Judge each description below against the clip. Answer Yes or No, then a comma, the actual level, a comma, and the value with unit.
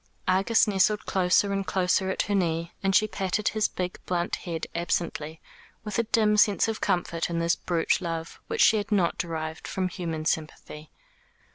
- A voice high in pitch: No, medium, 180 Hz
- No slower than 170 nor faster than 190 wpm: Yes, average, 175 wpm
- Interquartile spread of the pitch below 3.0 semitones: No, average, 3.3 semitones